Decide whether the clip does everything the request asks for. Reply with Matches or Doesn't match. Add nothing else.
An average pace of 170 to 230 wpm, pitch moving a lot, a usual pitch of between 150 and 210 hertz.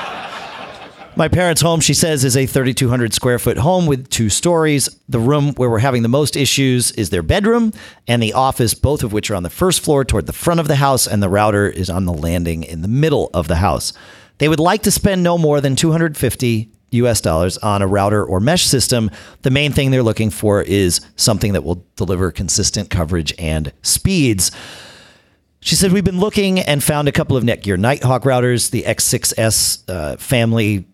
Doesn't match